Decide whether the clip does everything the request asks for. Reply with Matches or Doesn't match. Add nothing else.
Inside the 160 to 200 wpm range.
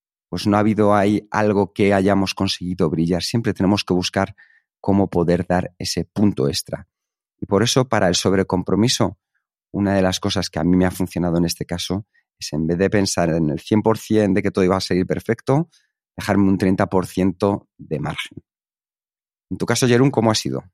Matches